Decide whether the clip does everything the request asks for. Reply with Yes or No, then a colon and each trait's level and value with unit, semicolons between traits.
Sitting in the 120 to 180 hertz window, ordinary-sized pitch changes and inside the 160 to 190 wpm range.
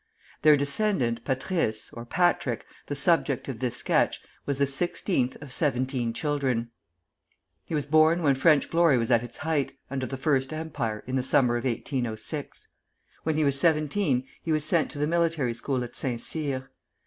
Yes: medium, 140 Hz; average, 3.9 semitones; average, 170 wpm